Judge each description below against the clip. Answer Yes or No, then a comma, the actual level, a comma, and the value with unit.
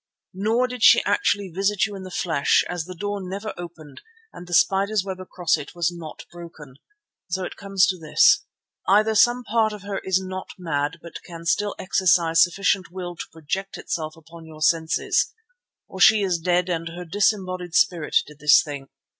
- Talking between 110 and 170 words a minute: No, average, 185 wpm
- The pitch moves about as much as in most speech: Yes, average, 3.1 semitones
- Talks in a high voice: No, medium, 180 Hz